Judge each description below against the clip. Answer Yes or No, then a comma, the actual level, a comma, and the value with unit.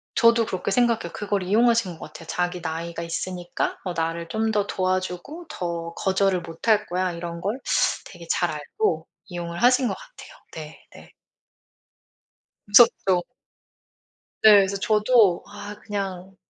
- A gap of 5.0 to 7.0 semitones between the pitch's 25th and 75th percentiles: No, average, 3.9 semitones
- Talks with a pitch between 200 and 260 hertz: No, high, 190 Hz